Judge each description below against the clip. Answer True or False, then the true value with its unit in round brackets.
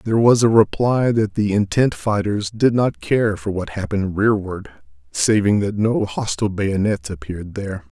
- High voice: False (100 Hz)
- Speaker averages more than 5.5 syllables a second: False (4.8 syllables/s)